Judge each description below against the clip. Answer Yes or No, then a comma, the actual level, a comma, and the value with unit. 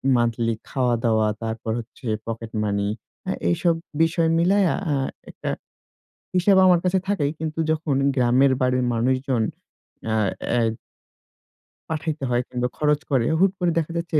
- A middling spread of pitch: No, wide, 5.7 semitones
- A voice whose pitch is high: No, low, 135 Hz